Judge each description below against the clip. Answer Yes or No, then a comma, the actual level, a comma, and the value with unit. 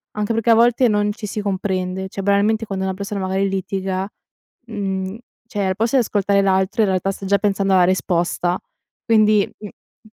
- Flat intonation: Yes, narrow, 1.9 semitones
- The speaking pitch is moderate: No, high, 200 Hz